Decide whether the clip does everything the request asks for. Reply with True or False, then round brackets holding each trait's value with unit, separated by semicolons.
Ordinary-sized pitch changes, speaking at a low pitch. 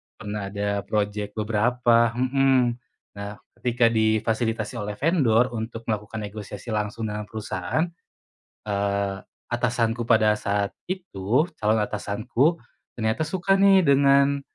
True (3.4 semitones; 110 Hz)